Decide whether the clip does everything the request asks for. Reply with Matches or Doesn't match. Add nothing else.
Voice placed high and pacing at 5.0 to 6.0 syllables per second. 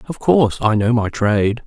Doesn't match